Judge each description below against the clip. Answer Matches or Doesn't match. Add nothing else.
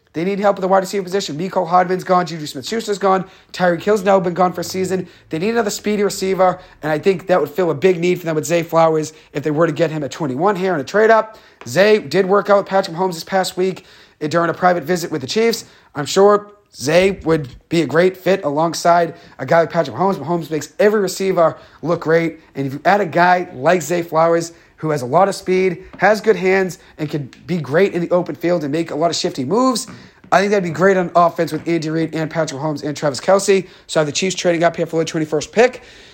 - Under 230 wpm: Doesn't match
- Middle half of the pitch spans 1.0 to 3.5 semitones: Matches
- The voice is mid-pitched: Matches